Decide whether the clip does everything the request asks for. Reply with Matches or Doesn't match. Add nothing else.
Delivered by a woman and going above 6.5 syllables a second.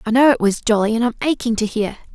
Matches